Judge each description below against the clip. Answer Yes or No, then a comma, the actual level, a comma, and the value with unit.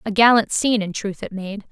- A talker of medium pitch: No, high, 210 Hz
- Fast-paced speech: Yes, fast, 245 wpm